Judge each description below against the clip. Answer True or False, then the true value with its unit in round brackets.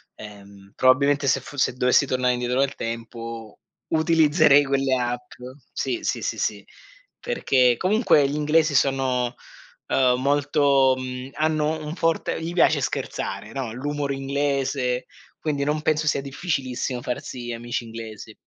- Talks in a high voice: False (135 Hz)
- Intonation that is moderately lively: True (3.0 semitones)